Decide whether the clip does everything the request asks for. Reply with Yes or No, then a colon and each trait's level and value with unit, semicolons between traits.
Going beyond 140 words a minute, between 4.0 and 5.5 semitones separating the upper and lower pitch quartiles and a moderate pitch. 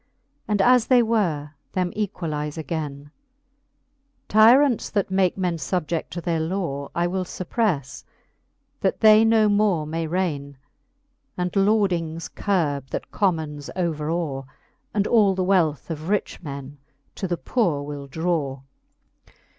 No: slow, 135 wpm; average, 4.9 semitones; medium, 175 Hz